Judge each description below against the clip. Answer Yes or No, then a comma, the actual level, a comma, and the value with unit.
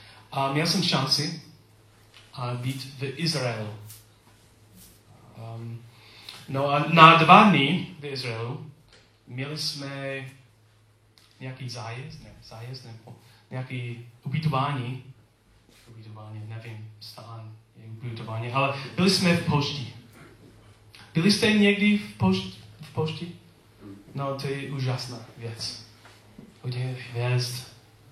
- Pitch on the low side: Yes, low, 120 Hz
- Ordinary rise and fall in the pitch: Yes, average, 3.9 semitones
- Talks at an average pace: No, slow, 100 wpm